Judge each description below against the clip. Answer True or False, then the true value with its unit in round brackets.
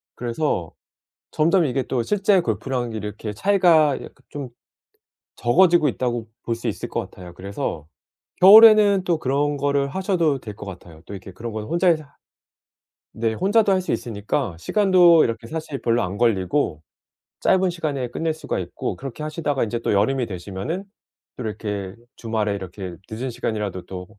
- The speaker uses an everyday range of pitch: False (7.7 semitones)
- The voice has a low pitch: True (125 Hz)